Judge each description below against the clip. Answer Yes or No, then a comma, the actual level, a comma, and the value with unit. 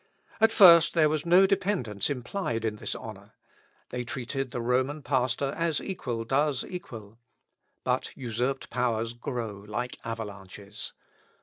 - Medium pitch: No, low, 125 Hz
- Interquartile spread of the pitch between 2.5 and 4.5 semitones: No, average, 5.0 semitones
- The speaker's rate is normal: No, slow, 130 wpm